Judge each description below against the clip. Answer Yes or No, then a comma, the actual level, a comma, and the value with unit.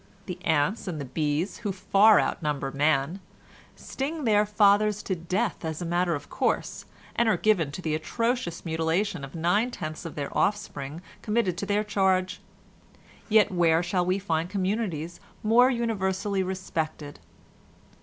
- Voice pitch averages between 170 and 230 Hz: Yes, medium, 185 Hz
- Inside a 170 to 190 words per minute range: No, average, 150 wpm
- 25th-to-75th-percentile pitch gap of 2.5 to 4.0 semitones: No, average, 4.5 semitones